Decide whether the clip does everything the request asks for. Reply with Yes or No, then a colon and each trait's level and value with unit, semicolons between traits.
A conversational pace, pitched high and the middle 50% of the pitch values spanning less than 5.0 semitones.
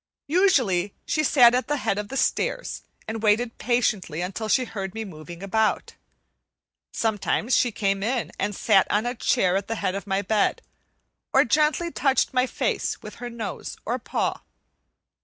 Yes: average, 170 wpm; high, 220 Hz; average, 4.2 semitones